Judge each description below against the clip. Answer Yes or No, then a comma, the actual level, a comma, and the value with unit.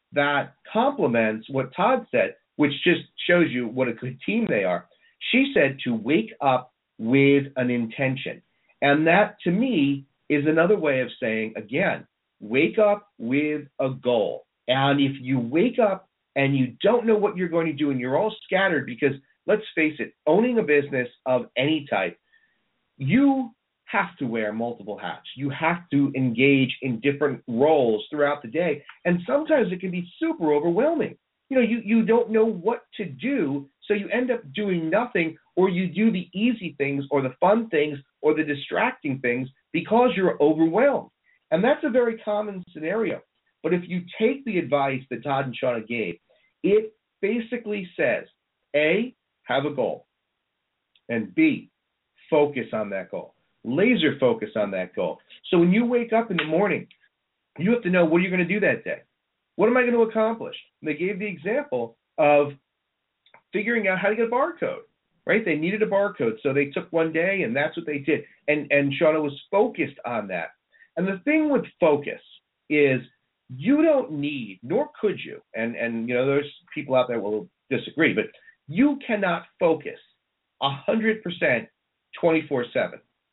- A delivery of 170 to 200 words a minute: Yes, average, 175 wpm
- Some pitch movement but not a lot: No, wide, 7.6 semitones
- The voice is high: No, medium, 165 Hz